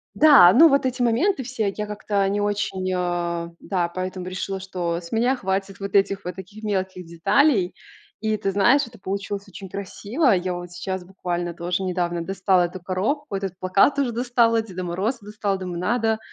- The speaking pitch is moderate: No, high, 195 Hz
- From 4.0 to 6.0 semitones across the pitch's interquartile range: No, average, 3.4 semitones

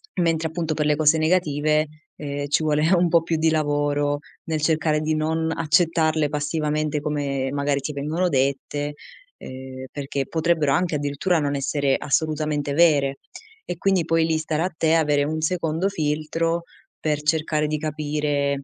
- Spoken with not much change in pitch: Yes, narrow, 1.8 semitones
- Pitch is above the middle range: No, medium, 155 Hz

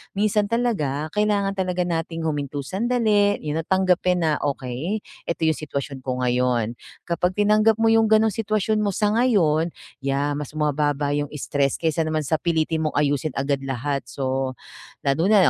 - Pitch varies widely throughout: Yes, wide, 6.1 semitones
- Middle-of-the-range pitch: Yes, medium, 160 Hz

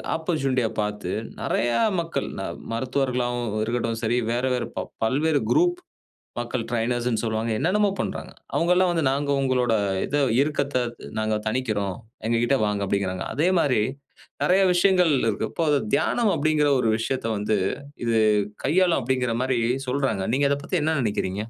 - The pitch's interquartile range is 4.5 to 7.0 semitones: Yes, average, 4.9 semitones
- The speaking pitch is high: No, low, 125 Hz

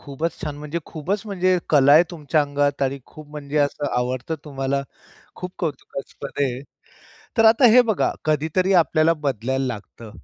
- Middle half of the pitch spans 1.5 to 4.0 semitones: Yes, average, 3.3 semitones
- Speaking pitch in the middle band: Yes, medium, 150 Hz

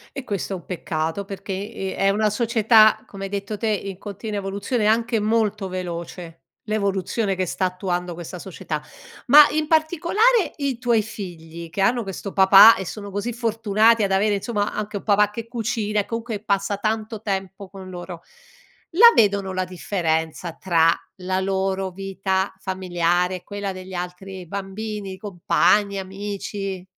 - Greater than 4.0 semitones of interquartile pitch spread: No, narrow, 2.6 semitones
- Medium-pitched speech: No, high, 200 Hz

